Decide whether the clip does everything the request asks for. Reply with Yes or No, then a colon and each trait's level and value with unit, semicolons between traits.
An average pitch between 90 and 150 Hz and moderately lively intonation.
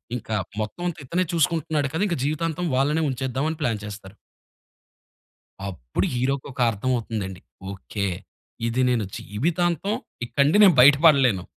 No: low, 135 Hz; wide, 6.6 semitones